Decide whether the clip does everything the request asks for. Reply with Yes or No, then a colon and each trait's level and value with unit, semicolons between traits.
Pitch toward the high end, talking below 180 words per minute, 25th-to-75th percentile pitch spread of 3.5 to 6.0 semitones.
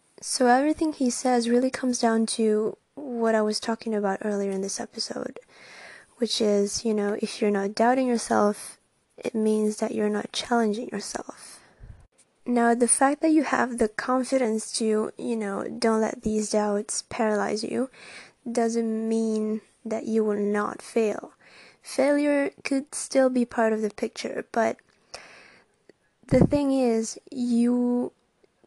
No: high, 230 Hz; average, 145 wpm; narrow, 2.4 semitones